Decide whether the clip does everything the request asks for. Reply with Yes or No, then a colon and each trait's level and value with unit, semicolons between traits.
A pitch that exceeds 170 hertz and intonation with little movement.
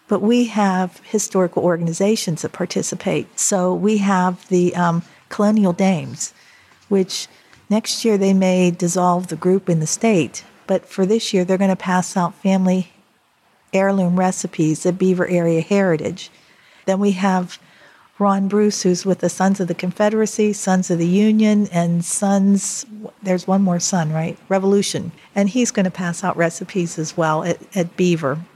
Yes: medium, 185 Hz; narrow, 2.3 semitones